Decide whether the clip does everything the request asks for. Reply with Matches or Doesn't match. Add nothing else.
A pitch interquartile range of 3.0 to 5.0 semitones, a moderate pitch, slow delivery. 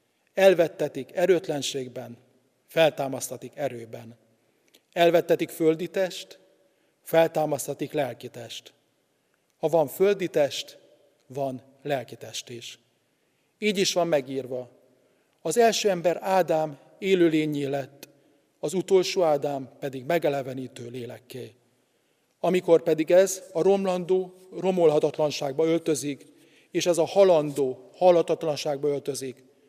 Matches